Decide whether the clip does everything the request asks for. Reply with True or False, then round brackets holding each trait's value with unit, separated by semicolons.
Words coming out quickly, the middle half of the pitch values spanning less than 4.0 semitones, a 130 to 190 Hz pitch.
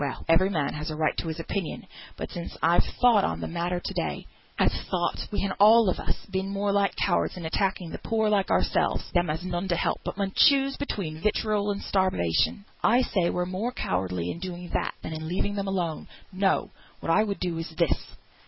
True (220 wpm; 3.5 semitones; 185 Hz)